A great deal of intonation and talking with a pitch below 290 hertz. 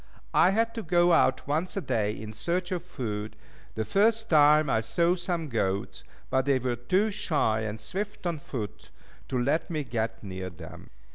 Yes: wide, 8.1 semitones; medium, 140 Hz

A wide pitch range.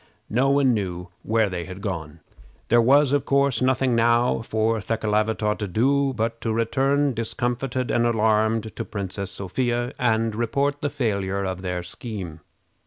No: average, 3.7 semitones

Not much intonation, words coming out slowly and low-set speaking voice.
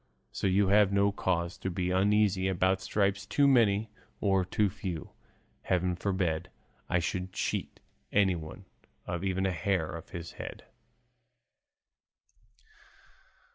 Yes: narrow, 2.1 semitones; slow, 125 wpm; very low, 95 Hz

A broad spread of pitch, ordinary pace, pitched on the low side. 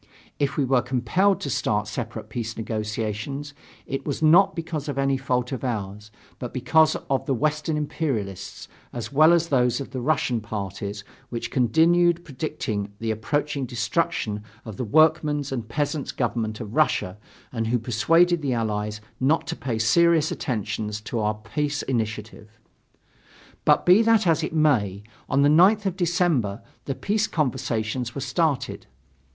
Yes: wide, 5.9 semitones; average, 155 wpm; low, 130 Hz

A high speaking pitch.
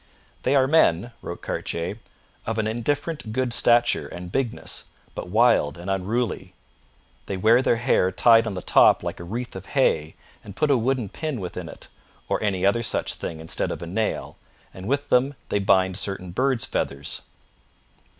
No: low, 110 Hz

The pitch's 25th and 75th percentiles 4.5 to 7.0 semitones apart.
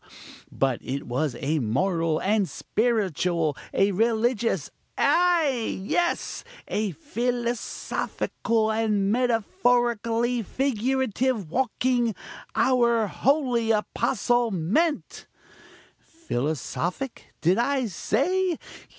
Yes: average, 4.8 semitones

